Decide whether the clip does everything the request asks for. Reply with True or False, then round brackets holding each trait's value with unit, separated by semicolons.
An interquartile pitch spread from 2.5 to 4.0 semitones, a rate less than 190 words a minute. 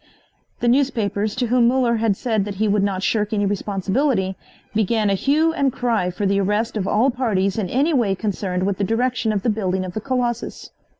False (3.6 semitones; 205 wpm)